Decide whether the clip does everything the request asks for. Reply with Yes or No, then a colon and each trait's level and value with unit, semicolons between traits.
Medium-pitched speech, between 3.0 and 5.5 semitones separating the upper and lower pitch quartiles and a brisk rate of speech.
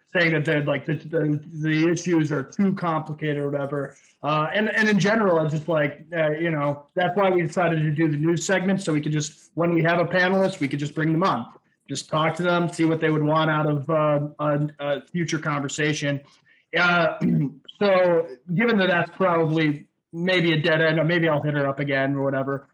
No: medium, 160 Hz; narrow, 2.6 semitones; fast, 220 wpm